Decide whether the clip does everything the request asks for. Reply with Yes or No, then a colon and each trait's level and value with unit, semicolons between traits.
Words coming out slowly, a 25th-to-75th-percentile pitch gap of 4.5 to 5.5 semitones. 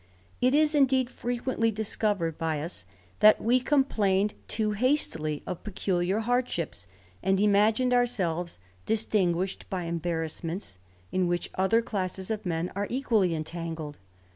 Yes: slow, 130 wpm; average, 5.1 semitones